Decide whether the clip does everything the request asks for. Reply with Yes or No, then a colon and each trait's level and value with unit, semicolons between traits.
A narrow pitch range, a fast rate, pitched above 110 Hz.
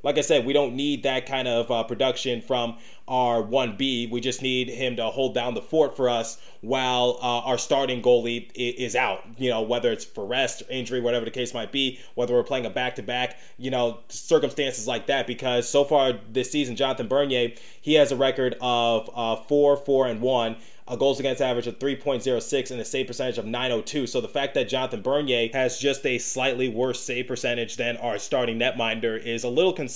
Yes: narrow, 1.8 semitones; fast, 210 wpm; low, 125 Hz